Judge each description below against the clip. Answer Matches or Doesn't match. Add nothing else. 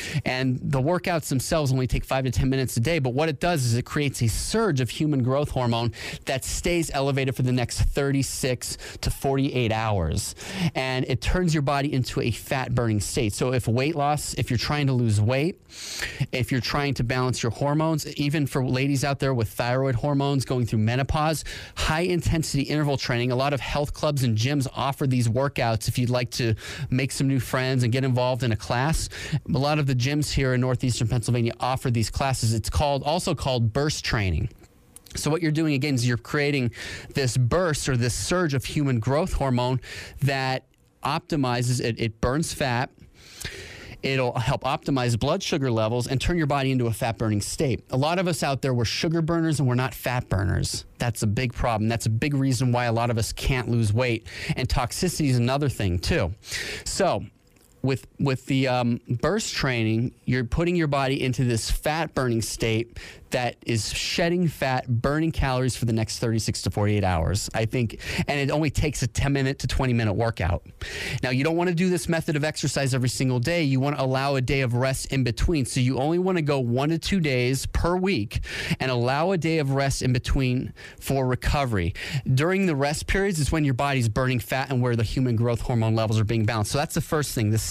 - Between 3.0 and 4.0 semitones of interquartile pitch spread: Matches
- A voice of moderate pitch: Doesn't match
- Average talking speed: Doesn't match